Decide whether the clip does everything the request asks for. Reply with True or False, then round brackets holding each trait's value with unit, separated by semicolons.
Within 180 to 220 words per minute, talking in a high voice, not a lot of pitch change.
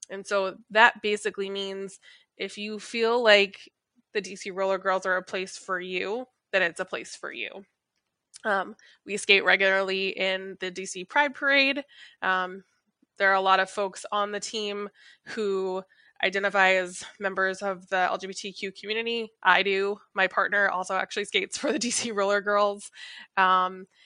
False (160 wpm; 195 Hz; 2.0 semitones)